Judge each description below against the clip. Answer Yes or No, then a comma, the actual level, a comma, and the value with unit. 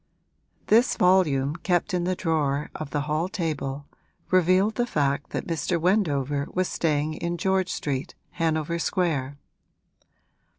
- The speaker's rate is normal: No, slow, 130 wpm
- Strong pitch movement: No, average, 4.0 semitones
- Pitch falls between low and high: Yes, medium, 165 Hz